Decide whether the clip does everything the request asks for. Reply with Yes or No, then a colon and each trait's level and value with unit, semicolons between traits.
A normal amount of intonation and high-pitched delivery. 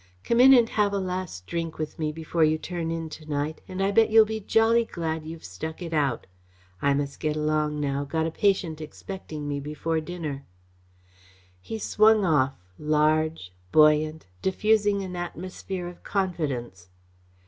No: average, 3.9 semitones; medium, 160 Hz